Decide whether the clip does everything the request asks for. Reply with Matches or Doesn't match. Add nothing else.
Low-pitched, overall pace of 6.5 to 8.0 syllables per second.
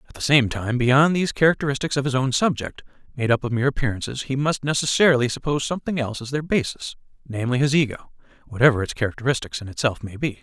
Matches